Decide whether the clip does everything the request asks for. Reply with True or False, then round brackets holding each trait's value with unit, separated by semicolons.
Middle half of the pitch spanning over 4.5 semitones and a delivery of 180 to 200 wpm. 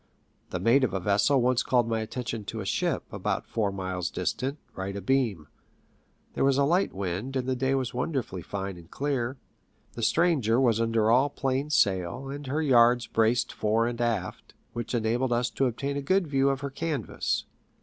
False (3.9 semitones; 190 wpm)